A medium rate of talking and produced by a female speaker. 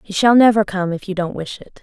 No: fast, 295 wpm; female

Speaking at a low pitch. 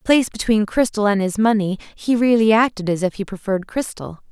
No: high, 210 Hz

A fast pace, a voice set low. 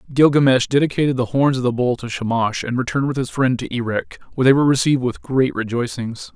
Yes: fast, 215 wpm; low, 125 Hz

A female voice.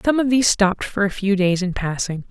Yes: female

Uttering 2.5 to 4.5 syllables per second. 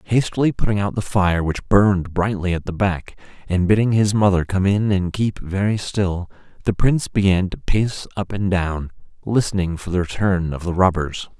No: 4.9 syllables/s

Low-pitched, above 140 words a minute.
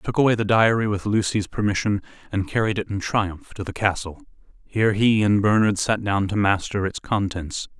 Yes: low, 100 Hz; average, 200 wpm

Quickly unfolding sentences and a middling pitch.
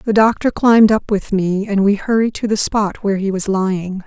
No: fast, 235 wpm; high, 205 Hz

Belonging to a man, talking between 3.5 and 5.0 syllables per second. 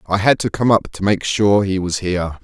No: male; 5.4 syllables/s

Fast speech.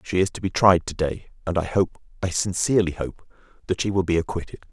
Yes: fast, 215 wpm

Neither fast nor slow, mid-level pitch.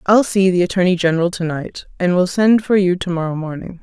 No: fast, 235 wpm; medium, 180 Hz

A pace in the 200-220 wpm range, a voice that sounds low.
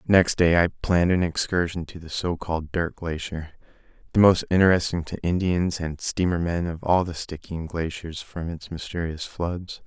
No: average, 170 wpm; very low, 85 Hz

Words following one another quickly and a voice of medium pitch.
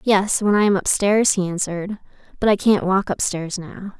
No: fast, 225 wpm; high, 195 Hz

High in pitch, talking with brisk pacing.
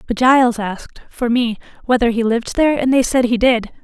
Yes: high, 240 Hz; fast, 220 wpm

